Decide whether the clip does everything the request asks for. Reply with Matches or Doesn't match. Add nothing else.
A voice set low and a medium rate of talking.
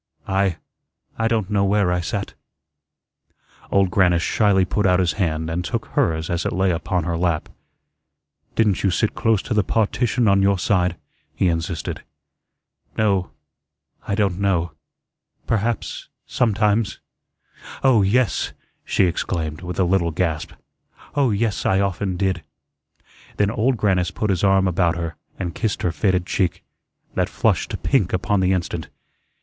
Matches